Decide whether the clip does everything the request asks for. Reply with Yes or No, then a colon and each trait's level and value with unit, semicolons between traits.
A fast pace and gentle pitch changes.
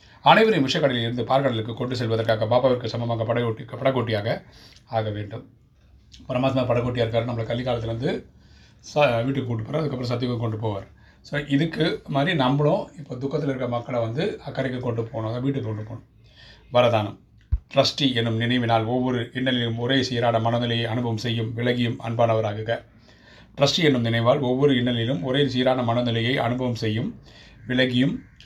Yes: fast, 135 wpm; narrow, 2.3 semitones